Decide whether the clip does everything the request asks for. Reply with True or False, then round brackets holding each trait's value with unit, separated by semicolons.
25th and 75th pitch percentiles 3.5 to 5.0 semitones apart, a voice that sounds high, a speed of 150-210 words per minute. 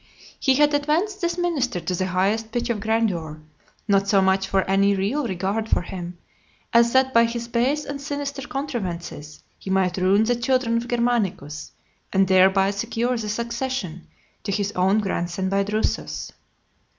True (4.4 semitones; 215 Hz; 165 wpm)